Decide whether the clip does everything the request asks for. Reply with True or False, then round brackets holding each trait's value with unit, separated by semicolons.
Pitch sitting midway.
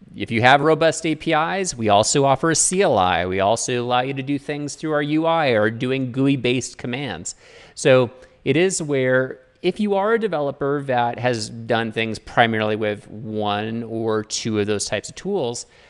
False (130 Hz)